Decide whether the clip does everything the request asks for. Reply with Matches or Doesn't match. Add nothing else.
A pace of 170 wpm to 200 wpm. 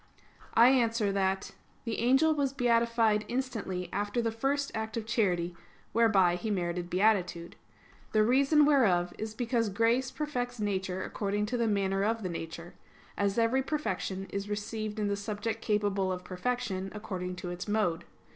Doesn't match